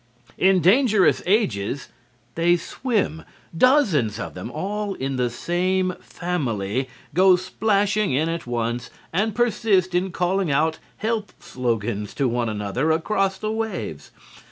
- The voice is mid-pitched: Yes, medium, 175 Hz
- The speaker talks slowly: Yes, slow, 130 wpm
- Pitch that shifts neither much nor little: No, wide, 8.0 semitones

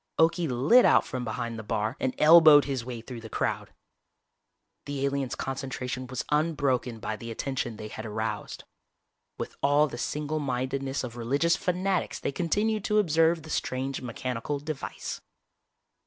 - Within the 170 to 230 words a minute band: No, average, 155 wpm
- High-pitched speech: No, low, 135 Hz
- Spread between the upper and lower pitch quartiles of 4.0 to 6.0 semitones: Yes, average, 4.3 semitones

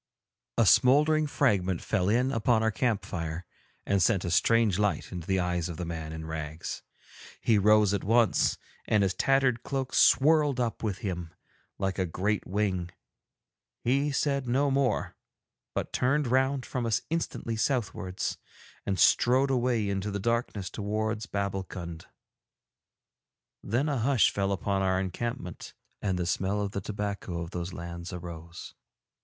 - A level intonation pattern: No, average, 5.1 semitones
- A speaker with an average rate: Yes, average, 150 wpm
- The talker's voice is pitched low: Yes, low, 105 Hz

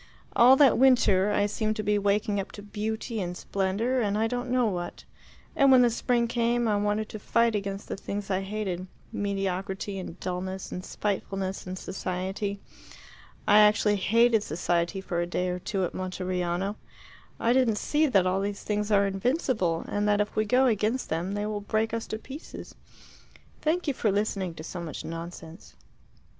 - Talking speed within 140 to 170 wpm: No, average, 180 wpm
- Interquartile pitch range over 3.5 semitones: No, average, 3.0 semitones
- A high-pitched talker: Yes, high, 205 Hz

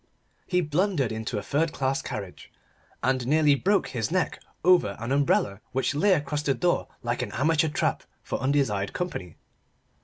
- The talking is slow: No, average, 160 wpm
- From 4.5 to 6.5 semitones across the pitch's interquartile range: Yes, wide, 5.5 semitones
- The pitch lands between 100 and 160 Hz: Yes, medium, 140 Hz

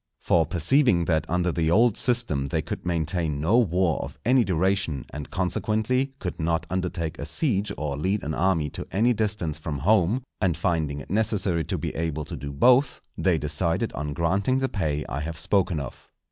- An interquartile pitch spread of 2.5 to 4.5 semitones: No, average, 5.1 semitones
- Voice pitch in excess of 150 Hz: No, very low, 85 Hz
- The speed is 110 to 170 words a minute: No, average, 190 wpm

